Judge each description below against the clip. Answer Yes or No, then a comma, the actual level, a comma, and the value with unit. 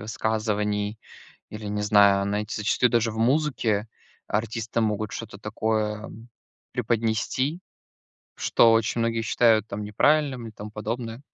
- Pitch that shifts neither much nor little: No, narrow, 1.7 semitones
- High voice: No, low, 110 Hz